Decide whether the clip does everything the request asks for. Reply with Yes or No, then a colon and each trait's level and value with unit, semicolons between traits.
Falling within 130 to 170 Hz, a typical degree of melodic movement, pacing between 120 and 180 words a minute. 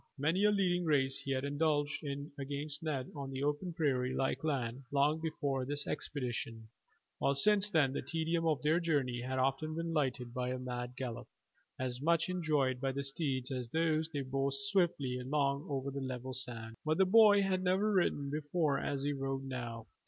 No: medium, 140 Hz; average, 3.5 semitones; average, 190 wpm